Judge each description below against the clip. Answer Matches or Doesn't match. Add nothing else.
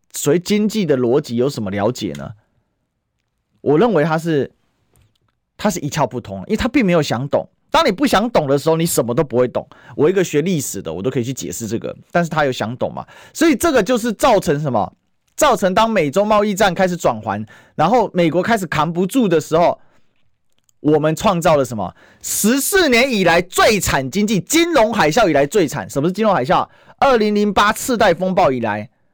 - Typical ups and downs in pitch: Doesn't match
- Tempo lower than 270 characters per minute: Doesn't match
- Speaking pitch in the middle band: Matches